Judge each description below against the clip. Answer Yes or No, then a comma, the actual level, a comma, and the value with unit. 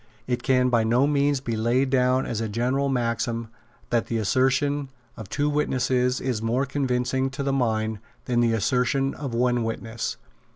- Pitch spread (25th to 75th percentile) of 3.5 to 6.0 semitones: No, narrow, 2.5 semitones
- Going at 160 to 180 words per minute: Yes, average, 170 wpm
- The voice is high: No, low, 125 Hz